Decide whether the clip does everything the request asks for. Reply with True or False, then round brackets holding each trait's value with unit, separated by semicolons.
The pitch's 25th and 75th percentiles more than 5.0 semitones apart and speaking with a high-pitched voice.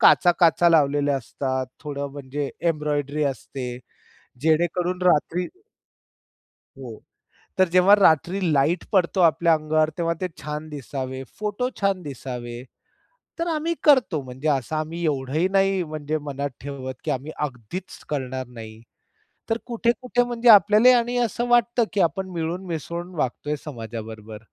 False (5.4 semitones; 155 Hz)